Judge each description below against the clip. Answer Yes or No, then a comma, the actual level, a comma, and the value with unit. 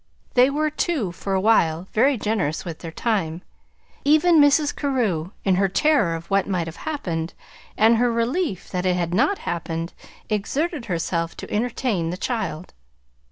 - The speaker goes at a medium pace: Yes, average, 160 wpm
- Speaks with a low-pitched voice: No, high, 200 Hz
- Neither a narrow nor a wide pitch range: No, wide, 7.6 semitones